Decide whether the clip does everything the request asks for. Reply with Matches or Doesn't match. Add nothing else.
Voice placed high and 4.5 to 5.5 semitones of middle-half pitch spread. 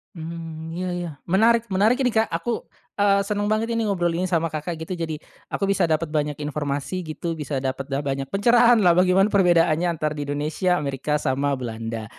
Doesn't match